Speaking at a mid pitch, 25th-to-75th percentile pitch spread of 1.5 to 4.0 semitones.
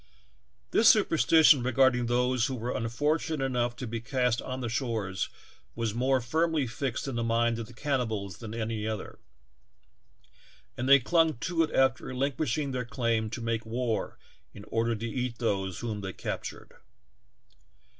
No: low, 120 Hz; average, 2.8 semitones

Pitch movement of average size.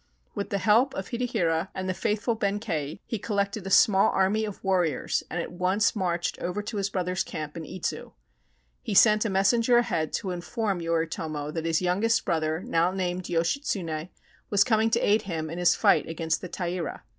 Yes: average, 3.8 semitones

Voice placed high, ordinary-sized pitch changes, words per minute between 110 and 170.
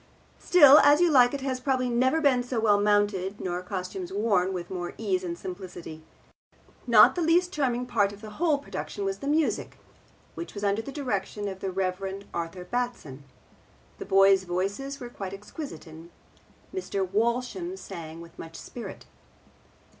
No: high, 205 Hz; wide, 5.7 semitones; average, 165 wpm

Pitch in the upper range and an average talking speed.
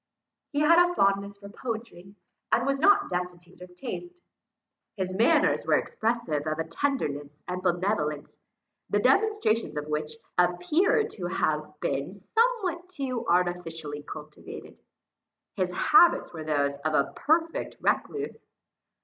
No: high, 195 Hz; slow, 130 wpm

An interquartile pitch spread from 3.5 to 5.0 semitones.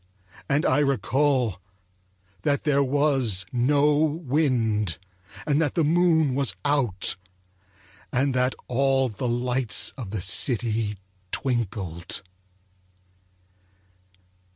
Yes: average, 4.6 semitones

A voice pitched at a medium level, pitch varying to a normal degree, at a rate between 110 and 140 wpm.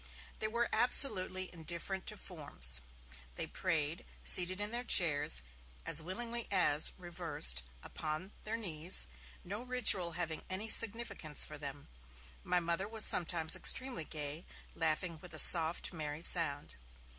Yes: medium, 175 Hz; average, 4.6 semitones; slow, 135 wpm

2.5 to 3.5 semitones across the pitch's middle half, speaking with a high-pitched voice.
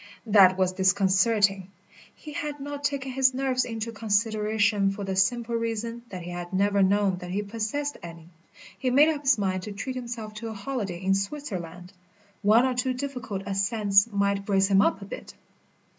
No: average, 4.2 semitones; high, 210 Hz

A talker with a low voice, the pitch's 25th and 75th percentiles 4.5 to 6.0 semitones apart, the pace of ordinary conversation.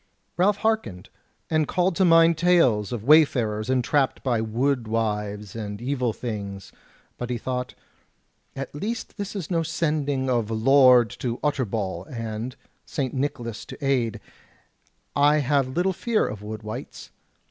Yes: low, 130 Hz; wide, 5.4 semitones; average, 145 wpm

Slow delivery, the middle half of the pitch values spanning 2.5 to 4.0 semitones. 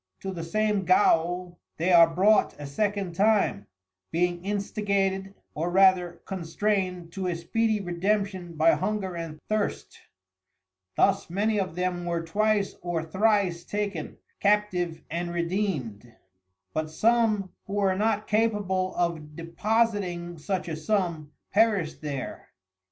Yes: slow, 125 wpm; average, 3.4 semitones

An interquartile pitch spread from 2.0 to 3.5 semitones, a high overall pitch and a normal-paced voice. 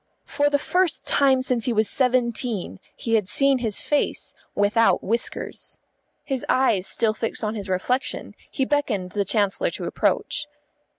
No: average, 4.4 semitones; high, 235 Hz; average, 155 wpm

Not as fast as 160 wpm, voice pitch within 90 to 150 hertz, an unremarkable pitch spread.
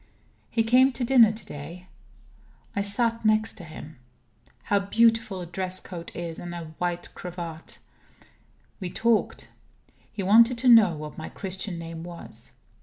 No: average, 150 wpm; high, 190 Hz; average, 4.8 semitones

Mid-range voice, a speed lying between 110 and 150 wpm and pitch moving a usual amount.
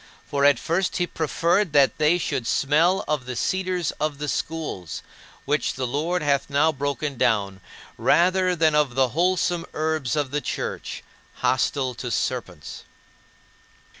Yes: medium, 150 Hz; average, 145 wpm; average, 3.9 semitones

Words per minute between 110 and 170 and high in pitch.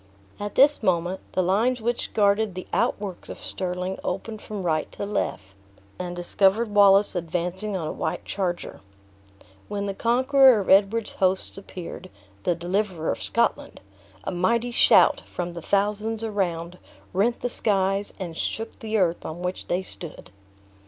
Yes: average, 150 wpm; high, 195 Hz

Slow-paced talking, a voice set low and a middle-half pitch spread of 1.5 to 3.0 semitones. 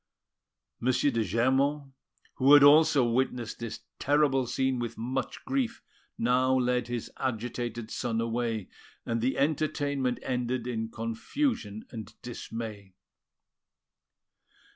Yes: slow, 110 wpm; low, 125 Hz; average, 2.7 semitones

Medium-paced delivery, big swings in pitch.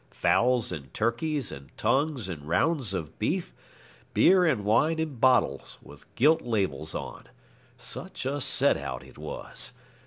Yes: average, 145 wpm; wide, 8.5 semitones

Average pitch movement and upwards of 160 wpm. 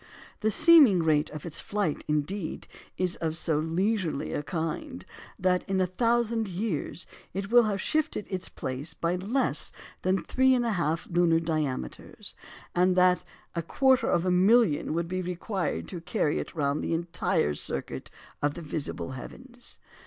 No: average, 4.8 semitones; average, 155 wpm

